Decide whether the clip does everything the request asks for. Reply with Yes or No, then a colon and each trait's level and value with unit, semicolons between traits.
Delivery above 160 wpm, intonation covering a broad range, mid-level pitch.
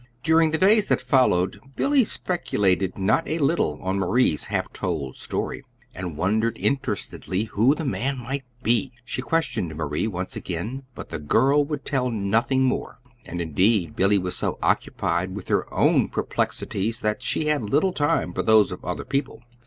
No: average, 170 wpm; wide, 7.0 semitones; low, 115 Hz